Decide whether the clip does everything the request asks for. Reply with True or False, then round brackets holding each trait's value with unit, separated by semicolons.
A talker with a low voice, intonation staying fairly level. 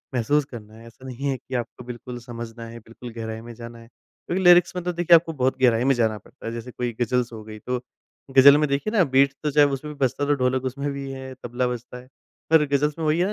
False (125 Hz; 3.3 semitones)